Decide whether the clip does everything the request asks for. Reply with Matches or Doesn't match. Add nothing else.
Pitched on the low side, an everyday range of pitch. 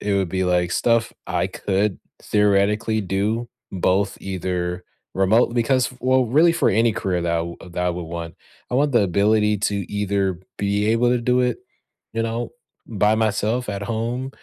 Matches